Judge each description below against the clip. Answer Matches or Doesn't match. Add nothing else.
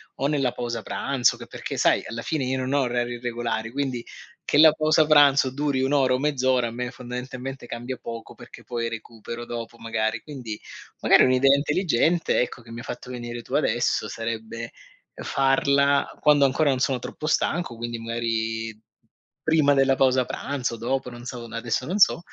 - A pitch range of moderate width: Matches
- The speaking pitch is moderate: Doesn't match